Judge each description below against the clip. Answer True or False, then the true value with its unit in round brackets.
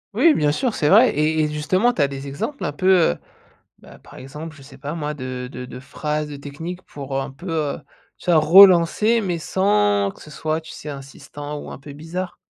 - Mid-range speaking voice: True (150 Hz)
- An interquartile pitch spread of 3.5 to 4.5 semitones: True (4.1 semitones)